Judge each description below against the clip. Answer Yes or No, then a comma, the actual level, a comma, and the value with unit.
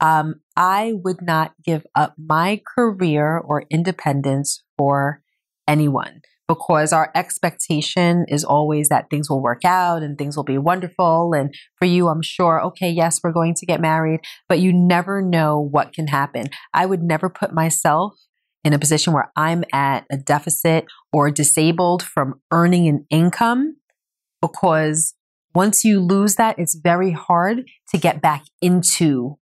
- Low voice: No, medium, 165 Hz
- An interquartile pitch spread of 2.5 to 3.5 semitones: Yes, average, 3.0 semitones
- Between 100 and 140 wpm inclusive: No, average, 155 wpm